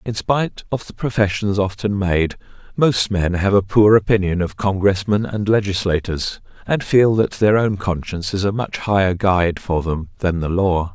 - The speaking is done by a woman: No, male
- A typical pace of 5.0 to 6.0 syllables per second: No, 4.8 syllables/s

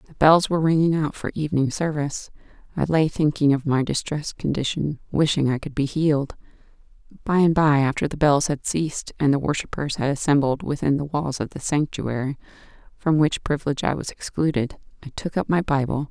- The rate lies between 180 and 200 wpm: Yes, average, 185 wpm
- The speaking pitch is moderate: Yes, medium, 145 Hz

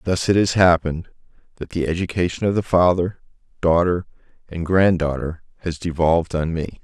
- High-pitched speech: No, very low, 85 Hz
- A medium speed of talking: Yes, average, 160 wpm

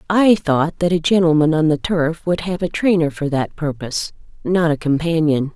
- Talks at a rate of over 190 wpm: No, average, 185 wpm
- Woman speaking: Yes, female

